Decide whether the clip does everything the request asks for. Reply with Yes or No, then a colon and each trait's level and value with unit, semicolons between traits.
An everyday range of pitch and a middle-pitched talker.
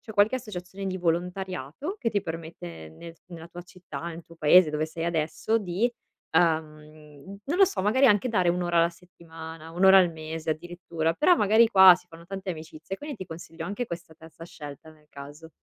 Yes: average, 3.2 semitones; medium, 170 Hz